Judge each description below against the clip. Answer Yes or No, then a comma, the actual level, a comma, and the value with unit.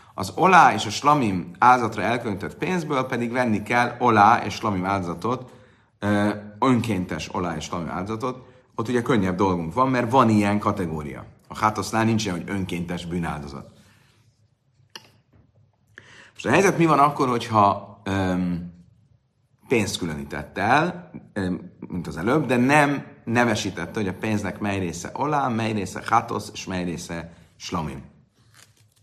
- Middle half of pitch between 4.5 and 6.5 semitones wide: Yes, average, 5.0 semitones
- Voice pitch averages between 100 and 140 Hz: Yes, low, 105 Hz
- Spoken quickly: No, average, 135 wpm